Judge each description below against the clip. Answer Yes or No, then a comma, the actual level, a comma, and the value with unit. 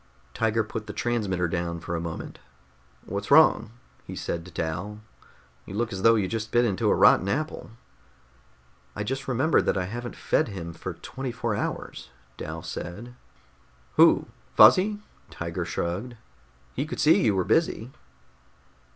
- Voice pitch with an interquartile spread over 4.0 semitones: Yes, average, 5.2 semitones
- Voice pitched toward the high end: No, low, 105 Hz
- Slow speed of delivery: No, average, 155 wpm